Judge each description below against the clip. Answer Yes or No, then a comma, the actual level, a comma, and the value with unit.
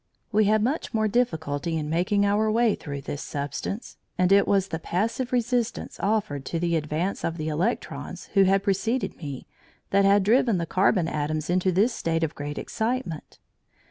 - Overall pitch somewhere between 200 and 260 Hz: No, high, 190 Hz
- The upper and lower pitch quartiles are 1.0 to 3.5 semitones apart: No, average, 5.1 semitones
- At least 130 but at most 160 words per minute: No, average, 175 wpm